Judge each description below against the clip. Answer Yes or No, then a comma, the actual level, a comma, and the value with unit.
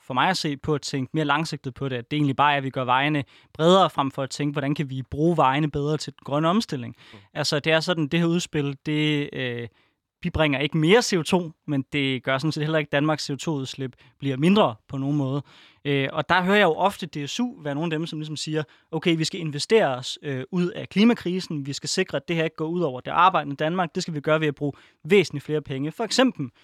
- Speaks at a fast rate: Yes, fast, 265 wpm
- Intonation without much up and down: No, average, 3.0 semitones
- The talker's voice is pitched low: No, medium, 150 Hz